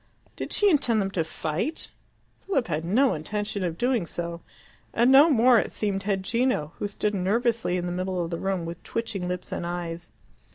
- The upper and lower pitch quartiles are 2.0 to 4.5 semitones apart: No, average, 5.1 semitones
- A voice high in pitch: Yes, high, 195 Hz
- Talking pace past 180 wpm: Yes, average, 195 wpm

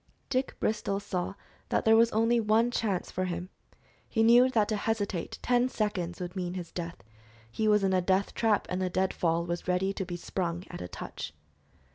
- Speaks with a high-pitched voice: Yes, high, 195 Hz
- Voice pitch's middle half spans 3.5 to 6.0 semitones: Yes, average, 3.8 semitones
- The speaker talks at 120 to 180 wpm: No, average, 200 wpm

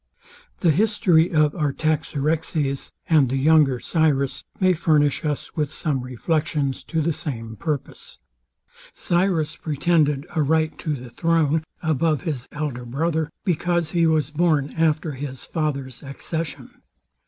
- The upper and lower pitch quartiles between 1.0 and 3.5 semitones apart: Yes, average, 2.7 semitones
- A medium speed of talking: No, slow, 130 wpm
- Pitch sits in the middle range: Yes, medium, 155 Hz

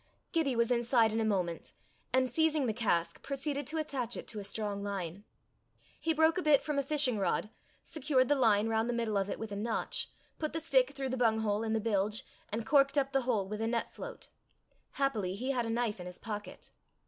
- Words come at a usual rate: No, fast, 220 wpm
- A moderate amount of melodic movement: Yes, average, 4.6 semitones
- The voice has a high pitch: Yes, high, 235 Hz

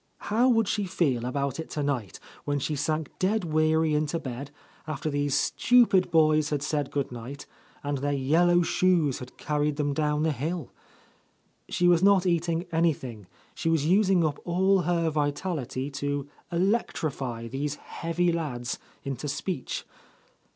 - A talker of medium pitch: Yes, medium, 155 Hz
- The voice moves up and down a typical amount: Yes, average, 3.5 semitones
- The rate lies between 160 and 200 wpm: No, average, 150 wpm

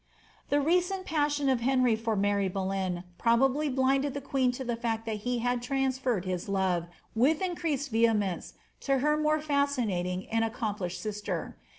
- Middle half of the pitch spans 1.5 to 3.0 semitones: No, wide, 5.4 semitones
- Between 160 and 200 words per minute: Yes, average, 165 wpm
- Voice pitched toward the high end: Yes, high, 245 Hz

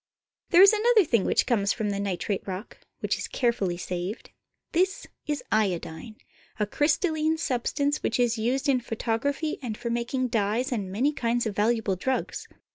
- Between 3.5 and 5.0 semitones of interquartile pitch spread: No, wide, 5.5 semitones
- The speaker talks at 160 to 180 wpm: Yes, average, 175 wpm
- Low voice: No, high, 235 Hz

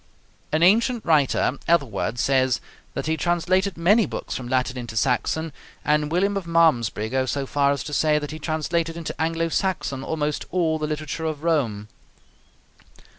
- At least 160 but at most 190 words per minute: Yes, average, 165 wpm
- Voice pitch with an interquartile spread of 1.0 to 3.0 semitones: No, average, 3.7 semitones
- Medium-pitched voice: Yes, medium, 155 Hz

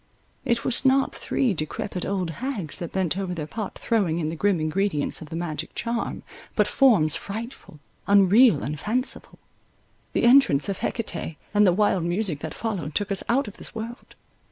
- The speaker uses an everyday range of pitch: No, wide, 5.8 semitones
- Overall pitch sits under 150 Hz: No, high, 195 Hz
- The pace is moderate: Yes, average, 180 wpm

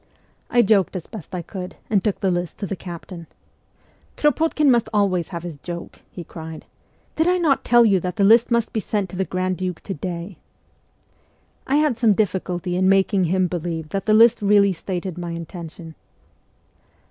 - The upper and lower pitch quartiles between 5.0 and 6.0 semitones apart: No, average, 3.7 semitones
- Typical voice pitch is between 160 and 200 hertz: Yes, high, 190 Hz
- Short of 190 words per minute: No, average, 200 wpm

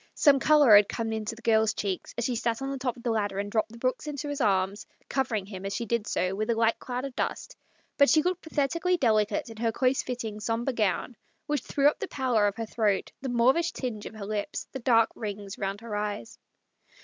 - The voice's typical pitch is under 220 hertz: No, high, 230 Hz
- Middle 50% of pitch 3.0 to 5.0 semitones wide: Yes, average, 4.0 semitones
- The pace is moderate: No, fast, 245 wpm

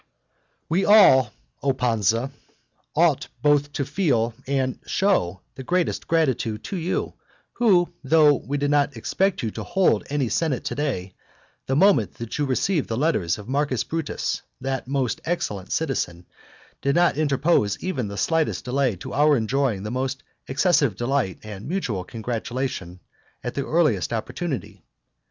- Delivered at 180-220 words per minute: No, average, 155 wpm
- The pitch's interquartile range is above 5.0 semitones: Yes, wide, 5.5 semitones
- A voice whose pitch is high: No, low, 135 Hz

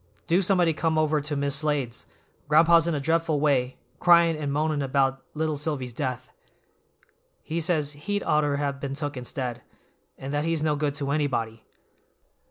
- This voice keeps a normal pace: Yes, average, 165 wpm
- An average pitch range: No, narrow, 2.3 semitones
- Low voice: No, medium, 150 Hz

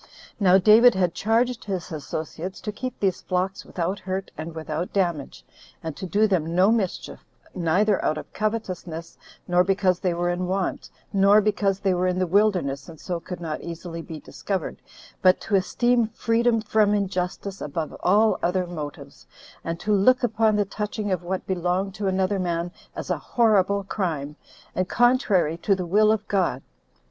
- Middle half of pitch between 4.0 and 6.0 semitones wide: No, average, 3.2 semitones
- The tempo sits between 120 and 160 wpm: No, average, 175 wpm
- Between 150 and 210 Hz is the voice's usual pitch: Yes, high, 190 Hz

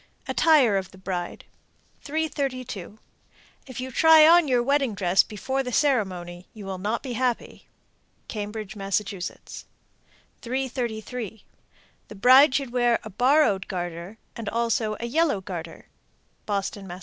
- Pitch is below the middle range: No, high, 225 Hz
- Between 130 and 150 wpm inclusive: Yes, slow, 135 wpm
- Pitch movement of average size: Yes, average, 5.0 semitones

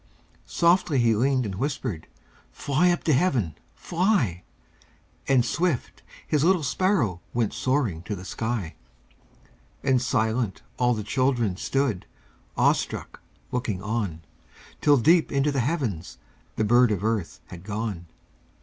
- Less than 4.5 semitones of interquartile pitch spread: No, wide, 5.4 semitones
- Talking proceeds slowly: Yes, slow, 130 wpm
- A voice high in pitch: No, low, 120 Hz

